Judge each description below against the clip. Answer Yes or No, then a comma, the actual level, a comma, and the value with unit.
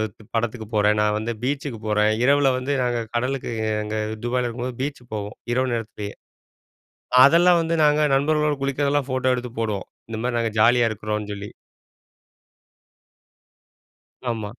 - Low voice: Yes, low, 120 Hz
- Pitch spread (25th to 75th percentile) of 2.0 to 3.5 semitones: No, average, 4.1 semitones